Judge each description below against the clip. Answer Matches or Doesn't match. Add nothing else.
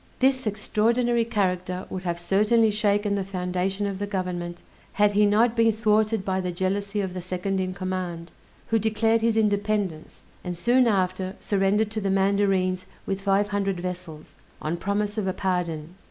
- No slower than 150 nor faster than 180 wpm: Matches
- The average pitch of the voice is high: Matches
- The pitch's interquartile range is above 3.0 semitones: Doesn't match